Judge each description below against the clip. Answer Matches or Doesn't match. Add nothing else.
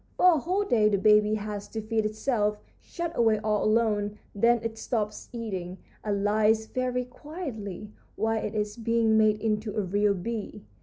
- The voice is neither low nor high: Doesn't match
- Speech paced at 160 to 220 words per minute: Matches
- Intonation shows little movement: Matches